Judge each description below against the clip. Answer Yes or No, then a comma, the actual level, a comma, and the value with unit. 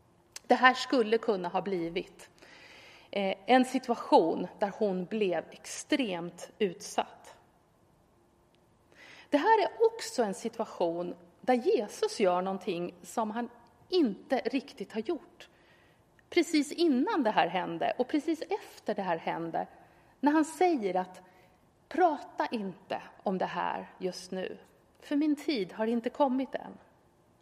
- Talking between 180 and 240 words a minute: No, slow, 125 wpm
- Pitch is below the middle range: No, high, 240 Hz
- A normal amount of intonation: No, wide, 7.9 semitones